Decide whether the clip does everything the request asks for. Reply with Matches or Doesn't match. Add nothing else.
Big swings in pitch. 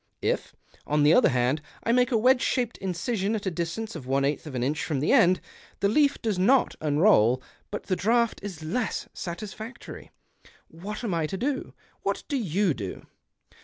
Matches